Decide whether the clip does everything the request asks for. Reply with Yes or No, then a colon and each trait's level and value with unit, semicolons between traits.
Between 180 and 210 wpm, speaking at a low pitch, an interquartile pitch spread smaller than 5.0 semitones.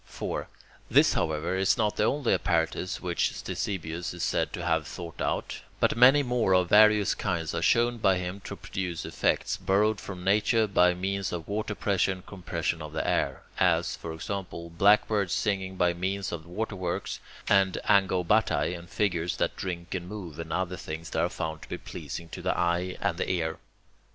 Yes: average, 185 wpm; very low, 90 Hz; average, 2.9 semitones